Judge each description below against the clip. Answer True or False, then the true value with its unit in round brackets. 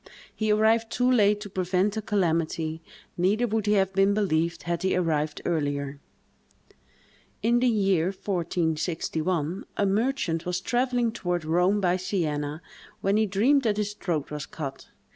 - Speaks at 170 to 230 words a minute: False (150 wpm)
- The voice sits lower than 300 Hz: True (185 Hz)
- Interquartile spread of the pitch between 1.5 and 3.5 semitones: False (4.3 semitones)